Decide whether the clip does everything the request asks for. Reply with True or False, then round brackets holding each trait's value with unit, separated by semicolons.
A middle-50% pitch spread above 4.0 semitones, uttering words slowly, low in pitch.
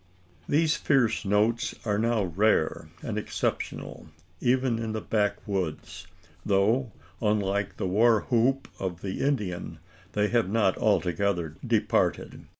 False (3.3 semitones; 120 wpm; 105 Hz)